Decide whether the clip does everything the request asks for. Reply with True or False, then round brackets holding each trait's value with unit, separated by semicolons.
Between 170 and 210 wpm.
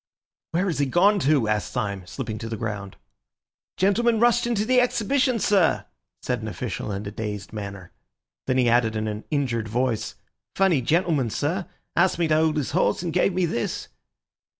True (180 wpm)